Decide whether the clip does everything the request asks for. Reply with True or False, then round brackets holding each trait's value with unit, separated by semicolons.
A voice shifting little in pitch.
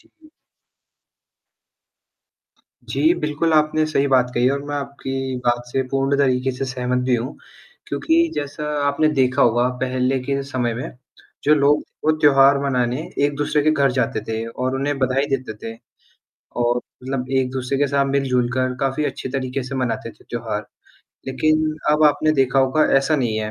True (2.1 semitones)